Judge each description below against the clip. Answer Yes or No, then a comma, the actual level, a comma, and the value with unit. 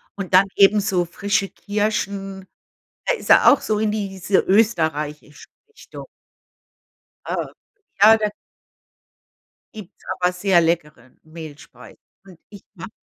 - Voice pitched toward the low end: No, high, 195 Hz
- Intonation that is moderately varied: Yes, average, 3.6 semitones